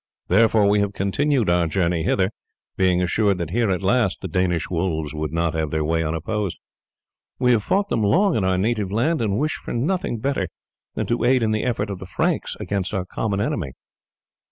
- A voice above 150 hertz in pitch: No, low, 100 Hz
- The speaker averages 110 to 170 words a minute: No, fast, 205 wpm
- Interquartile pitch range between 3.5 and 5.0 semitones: Yes, average, 4.6 semitones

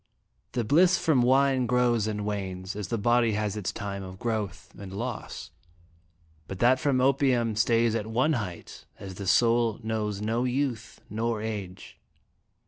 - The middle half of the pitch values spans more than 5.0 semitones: No, average, 3.2 semitones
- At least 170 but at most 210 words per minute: No, average, 160 wpm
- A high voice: No, low, 115 Hz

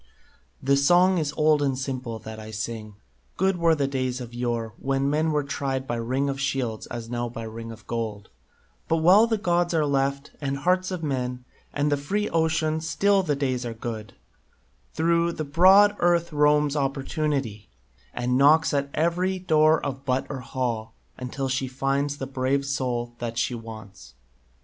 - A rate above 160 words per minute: Yes, average, 175 wpm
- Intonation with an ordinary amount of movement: Yes, average, 4.5 semitones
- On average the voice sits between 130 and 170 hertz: Yes, medium, 140 Hz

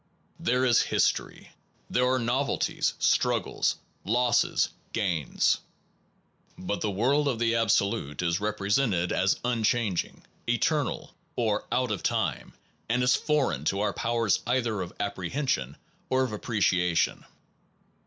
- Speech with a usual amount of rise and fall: Yes, average, 4.4 semitones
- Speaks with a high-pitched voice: No, low, 115 Hz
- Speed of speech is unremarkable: No, slow, 120 wpm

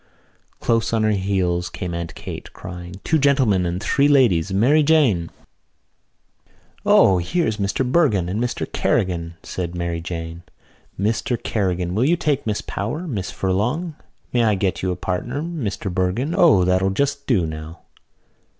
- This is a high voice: No, low, 100 Hz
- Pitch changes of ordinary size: No, wide, 6.7 semitones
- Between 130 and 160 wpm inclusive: Yes, average, 150 wpm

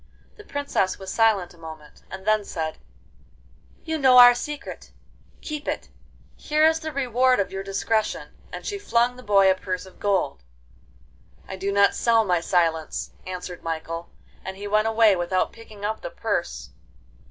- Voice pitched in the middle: No, high, 205 Hz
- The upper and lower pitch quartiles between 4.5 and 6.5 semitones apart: Yes, average, 4.9 semitones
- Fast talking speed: No, average, 165 wpm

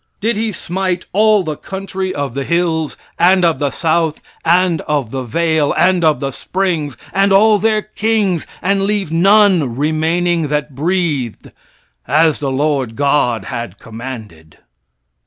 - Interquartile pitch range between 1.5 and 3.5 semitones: No, average, 5.0 semitones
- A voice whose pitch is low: No, medium, 165 Hz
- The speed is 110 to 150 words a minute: Yes, average, 145 wpm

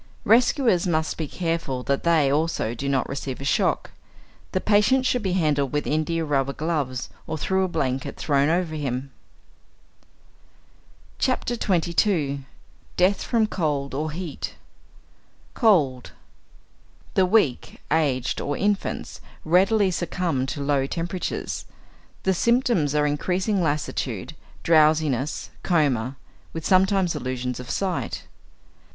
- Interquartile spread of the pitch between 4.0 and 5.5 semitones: Yes, average, 5.1 semitones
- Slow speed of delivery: Yes, slow, 120 wpm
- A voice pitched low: No, medium, 160 Hz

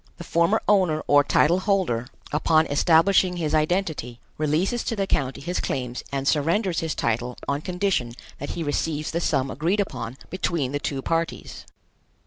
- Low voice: No, medium, 155 Hz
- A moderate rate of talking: Yes, average, 160 wpm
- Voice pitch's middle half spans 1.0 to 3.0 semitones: No, average, 4.3 semitones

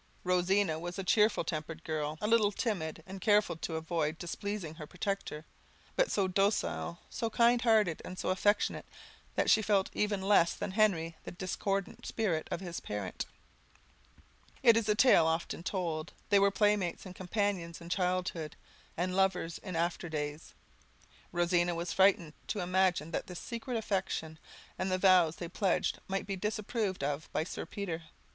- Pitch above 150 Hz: Yes, medium, 185 Hz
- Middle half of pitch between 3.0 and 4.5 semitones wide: Yes, average, 3.6 semitones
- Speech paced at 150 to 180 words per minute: Yes, average, 165 wpm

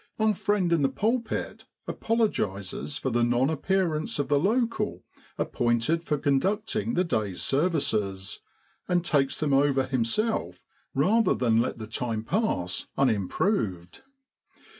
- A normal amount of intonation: No, wide, 8.7 semitones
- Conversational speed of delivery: No, slow, 130 wpm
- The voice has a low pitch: No, medium, 145 Hz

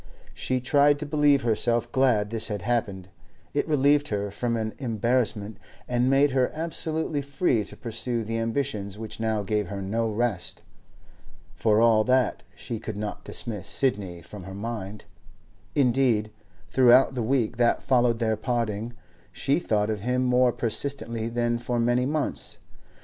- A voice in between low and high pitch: No, low, 120 Hz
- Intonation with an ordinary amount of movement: Yes, average, 3.3 semitones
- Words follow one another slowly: No, average, 155 wpm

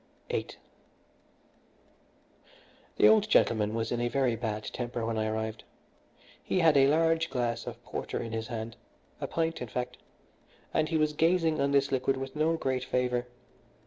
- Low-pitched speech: Yes, low, 130 Hz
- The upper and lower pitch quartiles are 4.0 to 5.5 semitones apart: Yes, average, 5.2 semitones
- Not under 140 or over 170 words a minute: Yes, average, 165 wpm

